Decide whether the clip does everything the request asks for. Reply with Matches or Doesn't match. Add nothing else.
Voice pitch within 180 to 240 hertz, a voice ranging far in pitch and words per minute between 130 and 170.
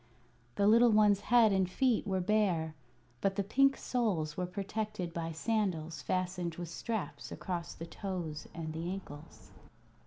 Doesn't match